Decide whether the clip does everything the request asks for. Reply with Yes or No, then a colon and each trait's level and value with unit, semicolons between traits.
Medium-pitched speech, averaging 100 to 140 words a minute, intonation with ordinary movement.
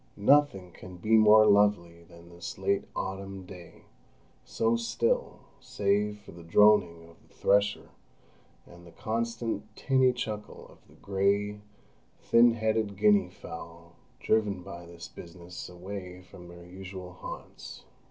No: low, 100 Hz; slow, 135 wpm; average, 3.4 semitones